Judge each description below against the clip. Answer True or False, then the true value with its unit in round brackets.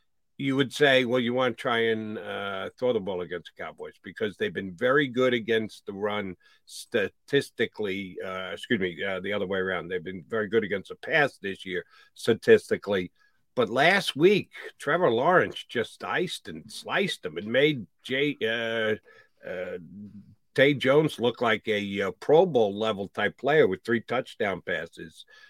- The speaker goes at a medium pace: True (170 wpm)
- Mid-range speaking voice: False (125 Hz)